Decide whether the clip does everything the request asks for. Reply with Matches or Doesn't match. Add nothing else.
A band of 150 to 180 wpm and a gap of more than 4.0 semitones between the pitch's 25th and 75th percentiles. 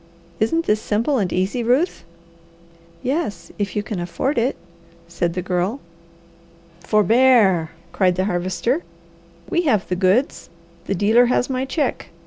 Doesn't match